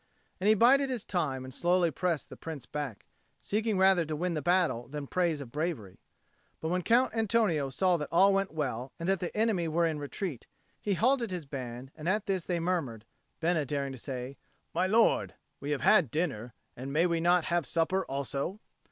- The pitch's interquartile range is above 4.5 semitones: Yes, average, 5.1 semitones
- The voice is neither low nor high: Yes, medium, 170 Hz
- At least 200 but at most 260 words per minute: Yes, fast, 205 wpm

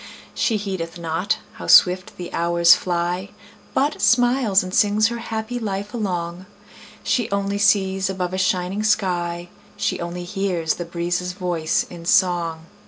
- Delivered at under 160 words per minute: Yes, average, 145 wpm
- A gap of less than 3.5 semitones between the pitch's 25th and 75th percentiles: Yes, average, 2.9 semitones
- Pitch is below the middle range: No, medium, 185 Hz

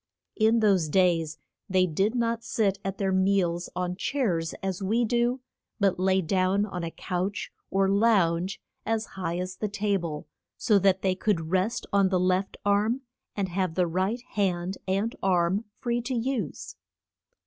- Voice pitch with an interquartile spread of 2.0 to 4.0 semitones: Yes, average, 2.8 semitones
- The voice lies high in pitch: Yes, high, 195 Hz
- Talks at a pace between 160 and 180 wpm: Yes, average, 165 wpm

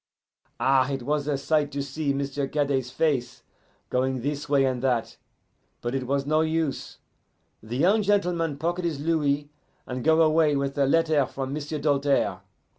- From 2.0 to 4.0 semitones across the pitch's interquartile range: Yes, narrow, 2.6 semitones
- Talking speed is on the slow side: No, average, 165 wpm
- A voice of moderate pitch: Yes, medium, 145 Hz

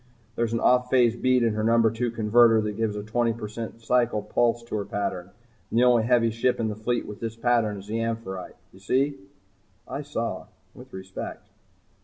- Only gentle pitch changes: Yes, narrow, 2.2 semitones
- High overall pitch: No, low, 115 Hz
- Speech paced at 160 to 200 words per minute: Yes, average, 190 wpm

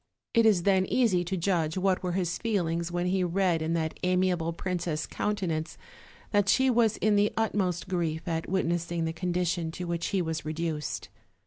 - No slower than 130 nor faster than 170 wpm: No, average, 180 wpm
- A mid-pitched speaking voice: Yes, medium, 180 Hz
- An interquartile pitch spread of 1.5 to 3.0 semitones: Yes, narrow, 2.6 semitones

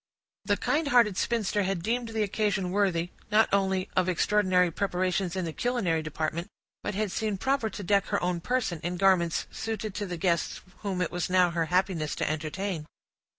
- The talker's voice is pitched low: No, high, 190 Hz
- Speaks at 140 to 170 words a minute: No, average, 185 wpm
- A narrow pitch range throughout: No, average, 3.1 semitones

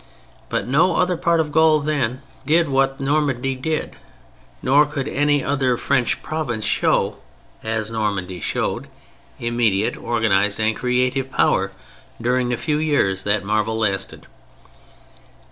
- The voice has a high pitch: No, low, 130 Hz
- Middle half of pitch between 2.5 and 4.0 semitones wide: No, average, 4.8 semitones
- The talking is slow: Yes, slow, 130 wpm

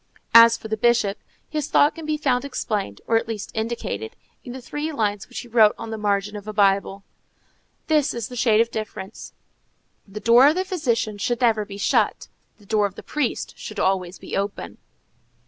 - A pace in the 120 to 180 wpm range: No, average, 200 wpm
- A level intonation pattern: No, average, 3.4 semitones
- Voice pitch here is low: No, high, 225 Hz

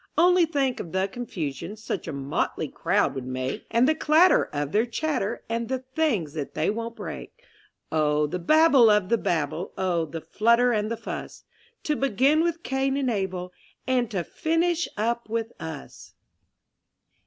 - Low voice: No, high, 225 Hz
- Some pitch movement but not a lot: No, wide, 8.0 semitones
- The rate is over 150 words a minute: Yes, average, 165 wpm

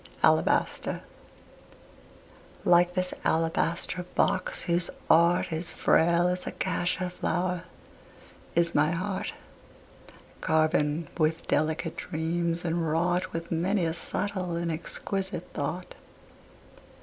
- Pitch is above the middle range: No, medium, 170 Hz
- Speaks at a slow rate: Yes, slow, 100 wpm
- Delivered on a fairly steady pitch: Yes, narrow, 1.7 semitones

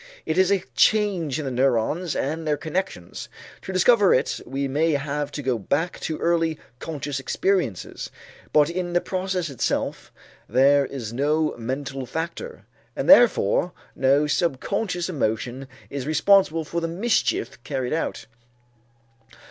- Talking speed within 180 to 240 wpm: No, average, 140 wpm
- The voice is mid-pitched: Yes, medium, 155 Hz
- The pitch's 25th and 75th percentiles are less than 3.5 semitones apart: No, average, 4.7 semitones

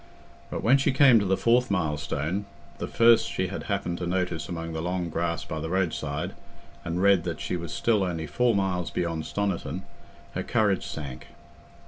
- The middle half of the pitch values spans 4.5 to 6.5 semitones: No, average, 3.4 semitones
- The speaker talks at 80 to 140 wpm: No, average, 180 wpm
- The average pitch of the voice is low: Yes, very low, 90 Hz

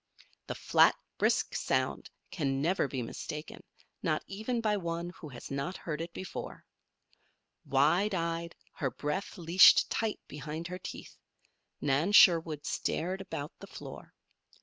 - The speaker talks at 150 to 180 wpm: No, slow, 135 wpm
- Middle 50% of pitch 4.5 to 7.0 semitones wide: No, average, 3.9 semitones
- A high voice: No, medium, 165 Hz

